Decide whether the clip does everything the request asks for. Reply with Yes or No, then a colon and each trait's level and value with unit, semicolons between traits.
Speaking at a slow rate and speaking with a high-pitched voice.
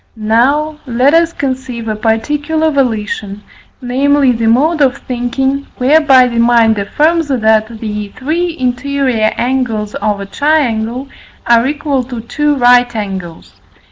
Yes: slow, 130 wpm; very high, 250 Hz